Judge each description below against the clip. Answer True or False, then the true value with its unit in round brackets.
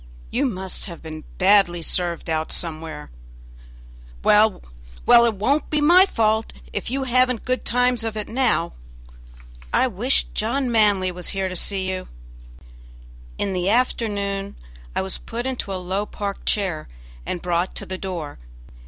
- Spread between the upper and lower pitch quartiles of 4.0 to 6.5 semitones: True (4.5 semitones)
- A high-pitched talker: True (200 Hz)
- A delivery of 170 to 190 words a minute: False (155 wpm)